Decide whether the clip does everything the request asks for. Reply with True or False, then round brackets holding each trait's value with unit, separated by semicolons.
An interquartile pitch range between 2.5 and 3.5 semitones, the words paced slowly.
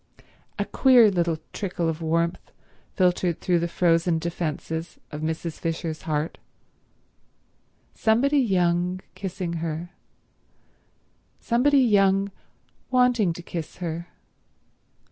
True (3.2 semitones; 95 wpm)